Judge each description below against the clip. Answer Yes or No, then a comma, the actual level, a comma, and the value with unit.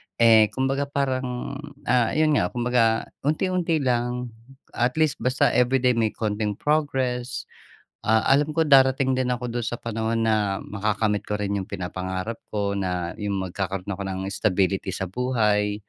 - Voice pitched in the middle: No, low, 115 Hz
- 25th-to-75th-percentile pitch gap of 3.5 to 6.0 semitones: Yes, average, 4.1 semitones